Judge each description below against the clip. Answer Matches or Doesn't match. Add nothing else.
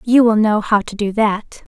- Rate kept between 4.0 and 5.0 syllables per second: Matches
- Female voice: Matches